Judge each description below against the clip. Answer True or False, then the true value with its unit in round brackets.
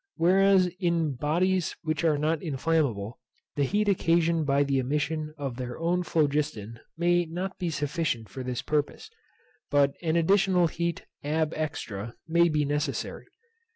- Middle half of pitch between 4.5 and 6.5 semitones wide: False (3.2 semitones)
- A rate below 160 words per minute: True (145 wpm)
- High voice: False (155 Hz)